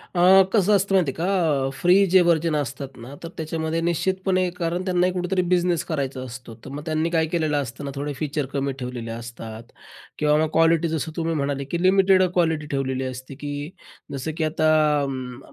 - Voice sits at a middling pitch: Yes, medium, 155 Hz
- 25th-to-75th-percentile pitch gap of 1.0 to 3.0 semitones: No, average, 4.1 semitones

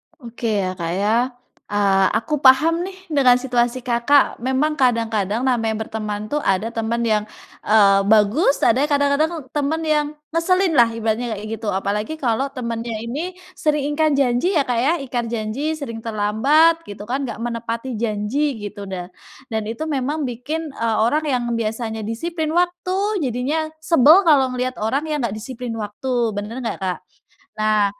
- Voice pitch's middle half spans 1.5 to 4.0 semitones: No, average, 5.0 semitones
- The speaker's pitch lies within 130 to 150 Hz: No, high, 240 Hz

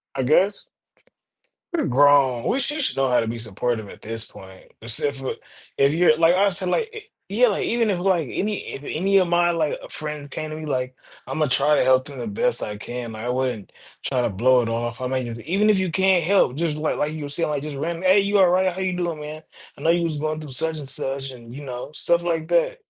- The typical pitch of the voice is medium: Yes, medium, 150 Hz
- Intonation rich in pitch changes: Yes, wide, 5.8 semitones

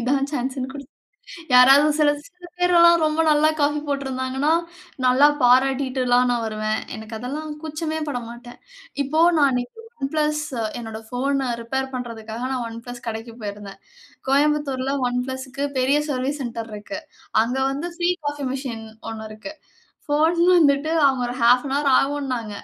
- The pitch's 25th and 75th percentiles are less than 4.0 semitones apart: Yes, average, 3.1 semitones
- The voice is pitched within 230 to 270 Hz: Yes, very high, 265 Hz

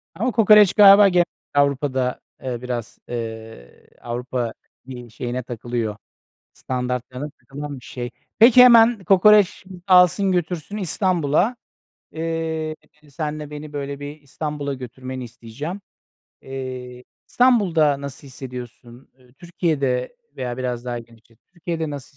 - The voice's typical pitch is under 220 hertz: Yes, medium, 140 Hz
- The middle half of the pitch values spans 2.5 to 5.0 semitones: No, wide, 5.6 semitones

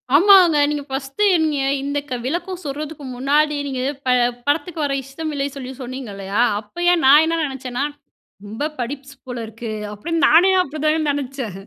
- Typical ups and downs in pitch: Yes, average, 3.4 semitones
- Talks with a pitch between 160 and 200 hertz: No, very high, 280 Hz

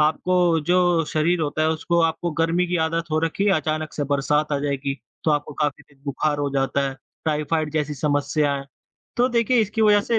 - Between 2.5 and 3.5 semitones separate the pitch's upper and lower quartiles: Yes, average, 2.9 semitones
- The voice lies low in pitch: No, medium, 155 Hz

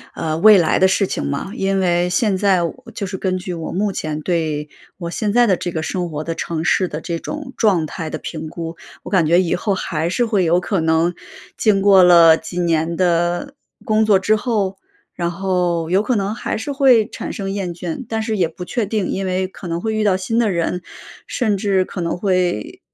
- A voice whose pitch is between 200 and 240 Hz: No, medium, 185 Hz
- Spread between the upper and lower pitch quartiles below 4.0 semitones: Yes, average, 3.4 semitones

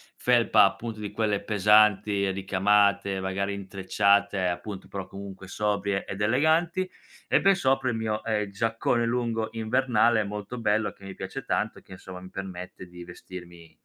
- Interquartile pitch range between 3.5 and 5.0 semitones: No, average, 2.7 semitones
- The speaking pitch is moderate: No, low, 105 Hz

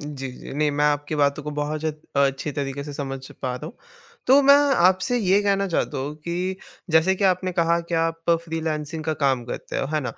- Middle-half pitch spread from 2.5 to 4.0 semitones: Yes, average, 3.3 semitones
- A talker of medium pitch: Yes, medium, 155 Hz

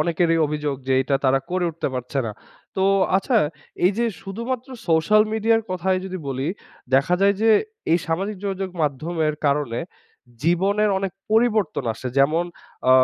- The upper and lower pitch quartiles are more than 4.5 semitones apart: Yes, average, 5.2 semitones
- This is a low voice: No, medium, 175 Hz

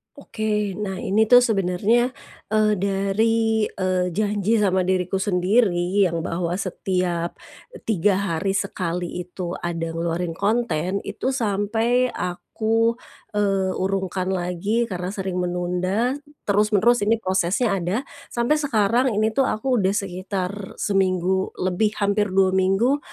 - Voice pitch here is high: Yes, high, 195 Hz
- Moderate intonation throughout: Yes, average, 3.1 semitones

